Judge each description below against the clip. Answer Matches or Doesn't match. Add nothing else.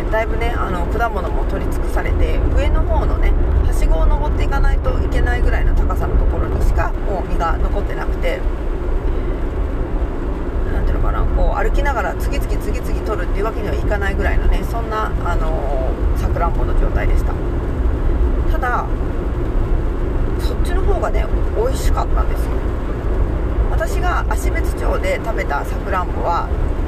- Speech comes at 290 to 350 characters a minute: Matches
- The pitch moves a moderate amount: Matches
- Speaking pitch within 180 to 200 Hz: Doesn't match